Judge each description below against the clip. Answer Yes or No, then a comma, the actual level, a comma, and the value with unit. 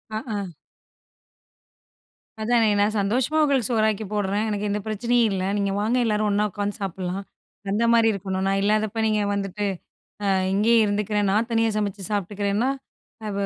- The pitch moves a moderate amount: No, narrow, 1.9 semitones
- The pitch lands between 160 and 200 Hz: No, high, 210 Hz